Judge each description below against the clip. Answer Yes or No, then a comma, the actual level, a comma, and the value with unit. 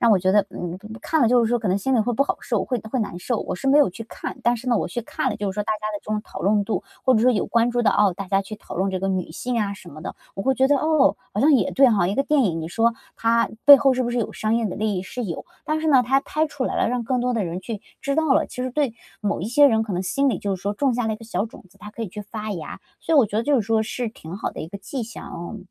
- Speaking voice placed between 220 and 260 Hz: Yes, high, 225 Hz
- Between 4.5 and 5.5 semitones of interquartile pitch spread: No, average, 4.1 semitones